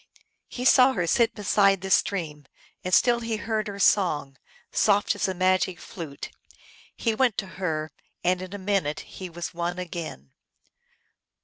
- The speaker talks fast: No, average, 155 wpm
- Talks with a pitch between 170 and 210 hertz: Yes, medium, 185 Hz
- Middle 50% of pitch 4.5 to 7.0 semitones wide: No, average, 3.2 semitones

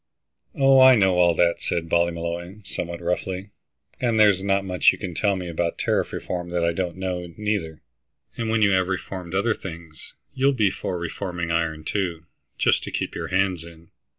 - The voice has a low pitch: Yes, very low, 90 Hz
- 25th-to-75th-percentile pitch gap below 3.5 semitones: Yes, average, 2.7 semitones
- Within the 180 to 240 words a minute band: Yes, average, 185 wpm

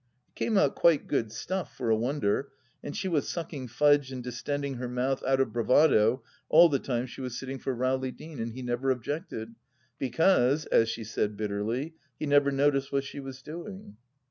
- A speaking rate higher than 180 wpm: Yes, average, 195 wpm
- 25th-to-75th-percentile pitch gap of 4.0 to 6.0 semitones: No, average, 3.2 semitones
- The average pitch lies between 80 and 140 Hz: Yes, low, 135 Hz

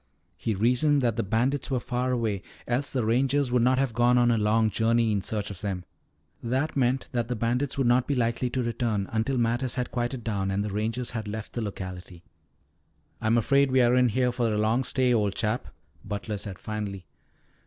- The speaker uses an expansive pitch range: No, average, 2.8 semitones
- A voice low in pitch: Yes, low, 120 Hz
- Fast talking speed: Yes, fast, 210 wpm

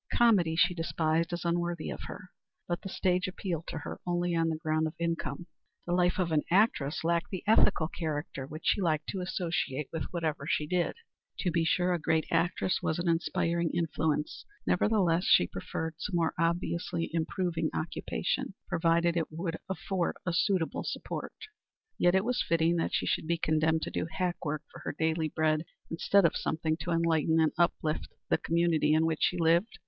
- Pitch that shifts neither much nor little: No, narrow, 1.8 semitones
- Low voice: No, medium, 165 Hz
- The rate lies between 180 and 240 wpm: Yes, average, 185 wpm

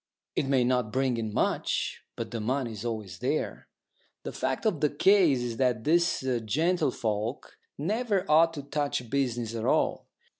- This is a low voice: Yes, low, 130 Hz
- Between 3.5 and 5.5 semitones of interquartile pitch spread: Yes, average, 4.8 semitones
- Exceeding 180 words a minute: No, average, 160 wpm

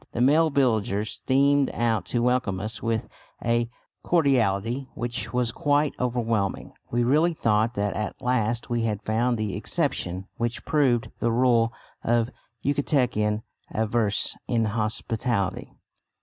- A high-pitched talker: No, low, 120 Hz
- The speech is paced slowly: Yes, slow, 130 wpm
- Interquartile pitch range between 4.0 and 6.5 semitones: No, average, 2.8 semitones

